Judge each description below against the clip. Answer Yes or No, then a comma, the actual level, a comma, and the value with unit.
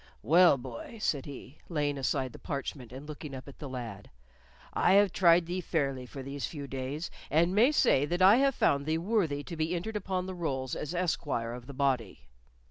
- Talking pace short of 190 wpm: No, fast, 205 wpm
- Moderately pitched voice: Yes, medium, 145 Hz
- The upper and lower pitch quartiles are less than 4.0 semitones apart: No, average, 4.9 semitones